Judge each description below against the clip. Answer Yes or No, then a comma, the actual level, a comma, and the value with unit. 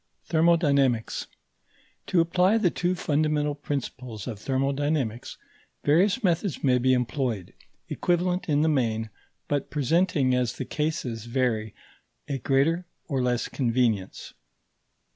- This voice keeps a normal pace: No, slow, 115 wpm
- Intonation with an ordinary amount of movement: Yes, average, 4.6 semitones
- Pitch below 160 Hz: Yes, medium, 140 Hz